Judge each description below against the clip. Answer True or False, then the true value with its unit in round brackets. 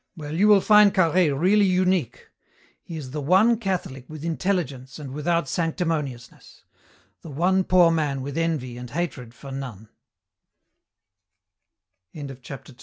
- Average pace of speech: False (120 wpm)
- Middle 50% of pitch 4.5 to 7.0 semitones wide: True (5.1 semitones)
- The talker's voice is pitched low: False (160 Hz)